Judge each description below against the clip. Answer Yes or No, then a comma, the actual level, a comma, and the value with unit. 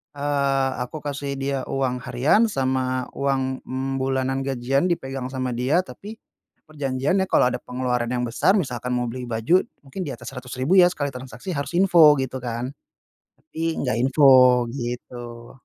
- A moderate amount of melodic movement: No, narrow, 2.3 semitones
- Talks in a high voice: No, low, 130 Hz